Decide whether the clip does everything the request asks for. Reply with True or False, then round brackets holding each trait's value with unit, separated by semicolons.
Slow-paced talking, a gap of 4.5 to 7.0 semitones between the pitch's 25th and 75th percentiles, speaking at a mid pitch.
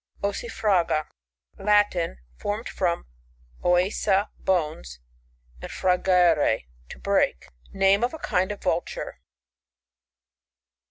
False (95 wpm; 3.7 semitones; 180 Hz)